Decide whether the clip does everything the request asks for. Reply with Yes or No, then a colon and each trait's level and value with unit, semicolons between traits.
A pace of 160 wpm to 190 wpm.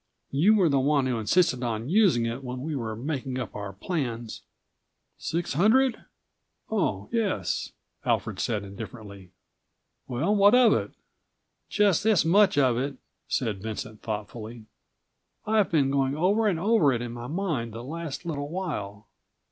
No: average, 150 wpm